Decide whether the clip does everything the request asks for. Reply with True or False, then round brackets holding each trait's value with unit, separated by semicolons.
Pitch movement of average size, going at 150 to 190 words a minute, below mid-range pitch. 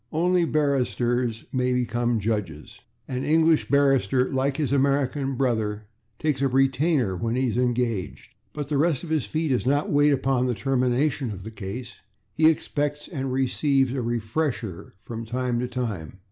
True (3.2 semitones; 160 wpm; 130 Hz)